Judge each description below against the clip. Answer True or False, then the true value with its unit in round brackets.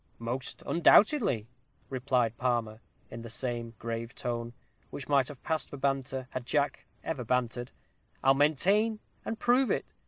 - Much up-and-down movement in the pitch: False (3.6 semitones)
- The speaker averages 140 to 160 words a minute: True (145 wpm)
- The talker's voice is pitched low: True (130 Hz)